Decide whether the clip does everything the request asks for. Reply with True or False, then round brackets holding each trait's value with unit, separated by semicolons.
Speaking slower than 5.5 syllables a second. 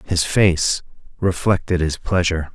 True (4.3 syllables/s)